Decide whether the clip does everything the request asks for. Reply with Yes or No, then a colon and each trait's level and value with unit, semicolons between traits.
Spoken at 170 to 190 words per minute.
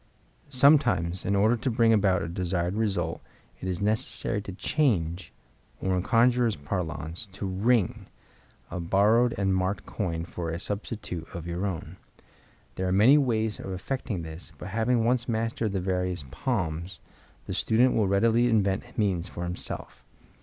No: average, 155 wpm